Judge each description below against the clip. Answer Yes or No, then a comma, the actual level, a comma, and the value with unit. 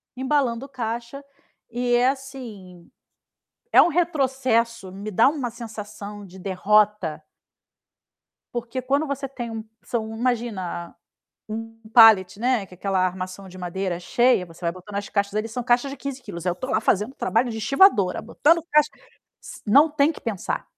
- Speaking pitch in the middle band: No, high, 225 Hz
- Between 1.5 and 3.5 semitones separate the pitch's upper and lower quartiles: No, average, 4.8 semitones